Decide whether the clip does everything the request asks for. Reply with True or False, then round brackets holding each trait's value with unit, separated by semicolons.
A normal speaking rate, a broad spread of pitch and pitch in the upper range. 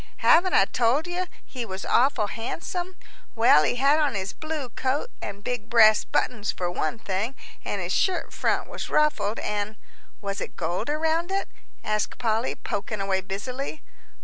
True (170 wpm; 6.8 semitones; 235 Hz)